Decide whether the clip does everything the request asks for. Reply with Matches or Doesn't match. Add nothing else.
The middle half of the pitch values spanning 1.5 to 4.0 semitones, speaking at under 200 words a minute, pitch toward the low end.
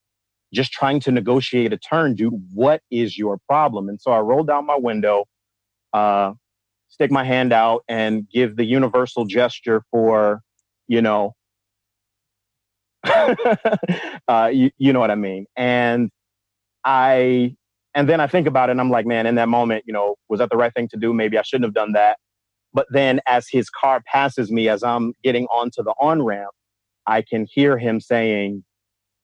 Matches